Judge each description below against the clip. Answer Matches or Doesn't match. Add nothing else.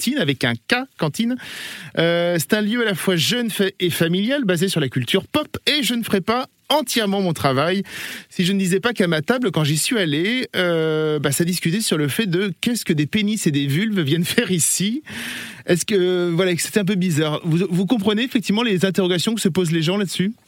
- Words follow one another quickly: Matches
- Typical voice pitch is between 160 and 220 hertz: Matches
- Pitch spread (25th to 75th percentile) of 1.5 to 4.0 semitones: Doesn't match